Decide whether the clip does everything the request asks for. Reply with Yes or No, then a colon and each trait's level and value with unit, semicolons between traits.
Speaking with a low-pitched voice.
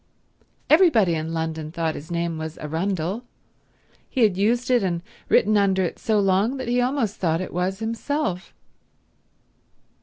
No: high, 190 Hz